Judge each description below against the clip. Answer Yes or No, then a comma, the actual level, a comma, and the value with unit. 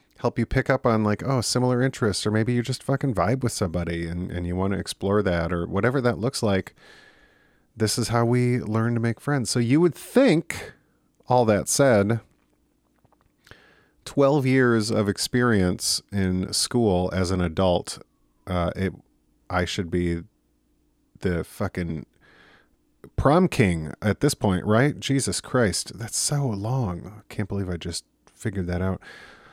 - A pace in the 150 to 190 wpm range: Yes, average, 160 wpm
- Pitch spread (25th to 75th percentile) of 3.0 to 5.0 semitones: No, wide, 5.4 semitones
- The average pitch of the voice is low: Yes, low, 105 Hz